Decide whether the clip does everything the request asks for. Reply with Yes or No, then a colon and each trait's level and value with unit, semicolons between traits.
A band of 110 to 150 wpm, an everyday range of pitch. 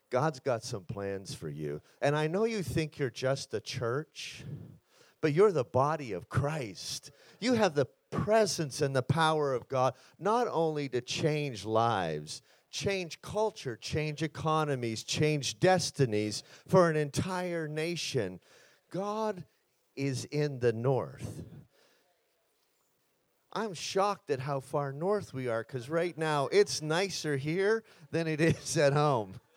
Yes: average, 140 wpm; average, 4.6 semitones